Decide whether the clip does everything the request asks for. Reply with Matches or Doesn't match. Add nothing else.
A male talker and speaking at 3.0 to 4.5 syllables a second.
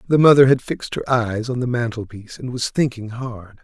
Doesn't match